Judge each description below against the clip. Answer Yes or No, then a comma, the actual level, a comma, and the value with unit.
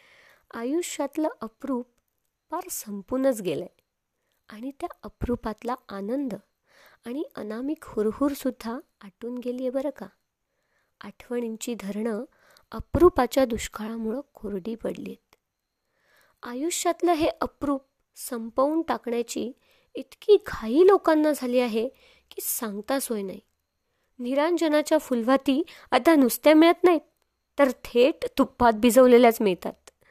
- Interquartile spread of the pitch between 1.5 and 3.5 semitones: No, average, 5.1 semitones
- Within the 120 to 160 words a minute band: No, average, 100 wpm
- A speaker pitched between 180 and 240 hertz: No, very high, 260 Hz